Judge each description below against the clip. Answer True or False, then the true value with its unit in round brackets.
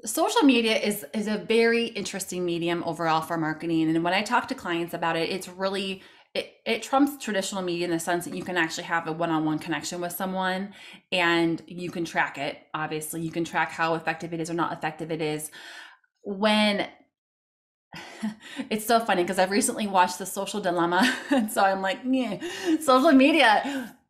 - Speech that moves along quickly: False (185 wpm)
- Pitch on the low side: False (185 Hz)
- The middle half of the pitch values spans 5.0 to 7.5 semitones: True (5.3 semitones)